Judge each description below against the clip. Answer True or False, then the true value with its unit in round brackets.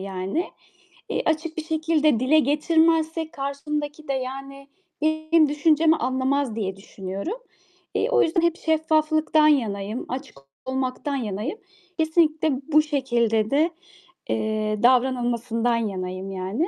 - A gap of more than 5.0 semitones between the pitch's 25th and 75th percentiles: True (5.4 semitones)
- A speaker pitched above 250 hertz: True (280 Hz)